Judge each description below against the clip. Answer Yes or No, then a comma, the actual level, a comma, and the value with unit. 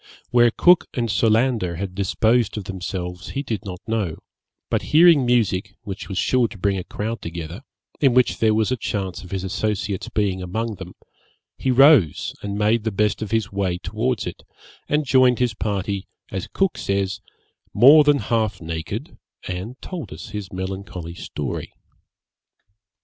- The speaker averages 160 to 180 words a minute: Yes, average, 165 wpm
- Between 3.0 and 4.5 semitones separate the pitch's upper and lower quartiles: Yes, average, 4.2 semitones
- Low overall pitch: Yes, low, 105 Hz